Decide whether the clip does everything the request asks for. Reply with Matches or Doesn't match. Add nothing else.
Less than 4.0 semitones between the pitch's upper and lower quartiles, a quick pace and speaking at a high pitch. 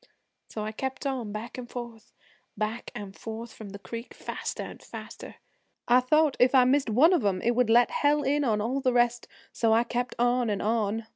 Matches